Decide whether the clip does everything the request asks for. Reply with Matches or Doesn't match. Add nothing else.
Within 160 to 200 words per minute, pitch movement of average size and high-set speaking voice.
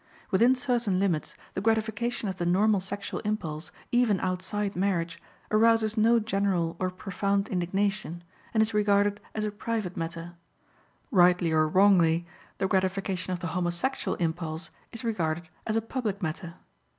Doesn't match